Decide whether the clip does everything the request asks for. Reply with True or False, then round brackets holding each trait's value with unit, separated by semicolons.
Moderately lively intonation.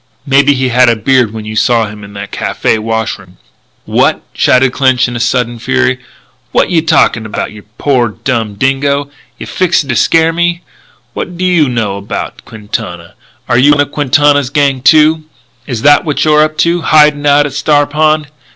True (4.6 semitones)